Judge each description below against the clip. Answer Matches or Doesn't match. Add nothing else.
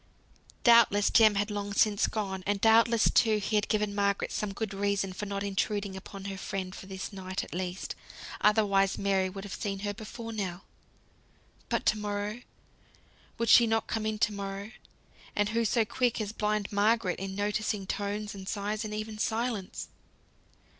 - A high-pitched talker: Matches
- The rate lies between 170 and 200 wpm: Matches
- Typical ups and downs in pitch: Doesn't match